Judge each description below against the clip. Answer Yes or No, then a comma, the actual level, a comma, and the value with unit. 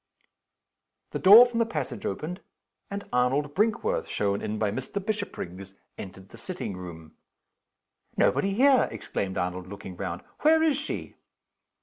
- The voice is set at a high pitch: No, low, 135 Hz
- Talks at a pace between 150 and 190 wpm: No, slow, 135 wpm